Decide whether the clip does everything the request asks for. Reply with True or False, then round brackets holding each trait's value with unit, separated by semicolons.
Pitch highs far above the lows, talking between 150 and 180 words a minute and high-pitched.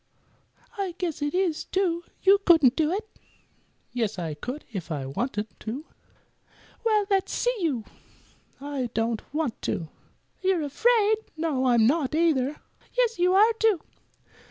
False (7.5 semitones; 140 wpm; 310 Hz)